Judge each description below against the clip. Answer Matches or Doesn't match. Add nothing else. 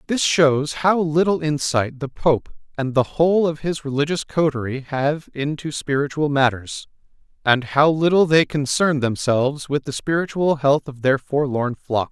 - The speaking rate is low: Doesn't match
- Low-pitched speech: Doesn't match